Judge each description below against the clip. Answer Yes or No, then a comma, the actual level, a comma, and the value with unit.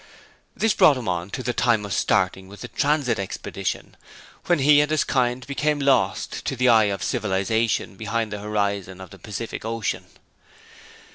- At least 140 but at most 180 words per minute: Yes, average, 170 wpm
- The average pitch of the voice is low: Yes, low, 115 Hz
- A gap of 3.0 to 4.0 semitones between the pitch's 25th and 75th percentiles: No, average, 4.7 semitones